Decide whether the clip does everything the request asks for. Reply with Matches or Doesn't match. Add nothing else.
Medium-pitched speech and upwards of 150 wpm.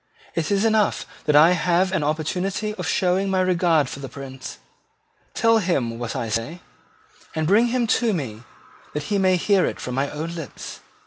Matches